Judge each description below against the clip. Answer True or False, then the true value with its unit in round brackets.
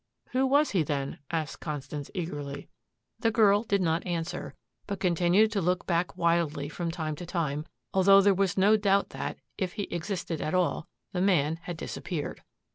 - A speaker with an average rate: True (175 wpm)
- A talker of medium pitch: True (175 Hz)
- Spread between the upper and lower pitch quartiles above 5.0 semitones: False (3.8 semitones)